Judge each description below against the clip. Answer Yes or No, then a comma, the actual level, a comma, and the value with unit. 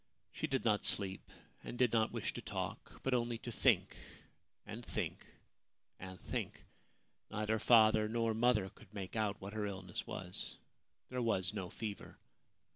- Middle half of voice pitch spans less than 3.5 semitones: Yes, average, 2.7 semitones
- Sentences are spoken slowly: No, average, 155 wpm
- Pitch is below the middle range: Yes, low, 110 Hz